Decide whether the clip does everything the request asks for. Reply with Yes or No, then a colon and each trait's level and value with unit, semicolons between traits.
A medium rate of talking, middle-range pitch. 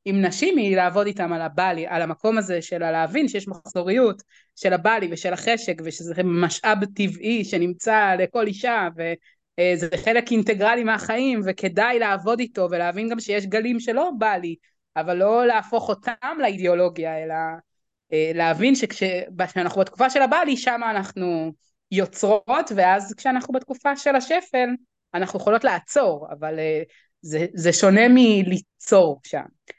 No: average, 130 wpm; high, 195 Hz